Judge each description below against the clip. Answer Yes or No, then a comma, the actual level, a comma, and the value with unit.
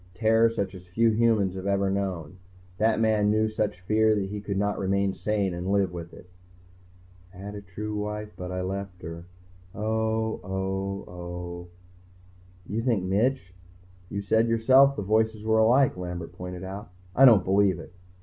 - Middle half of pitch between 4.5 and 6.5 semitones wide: No, average, 3.0 semitones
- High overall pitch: No, low, 100 Hz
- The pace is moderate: Yes, average, 170 wpm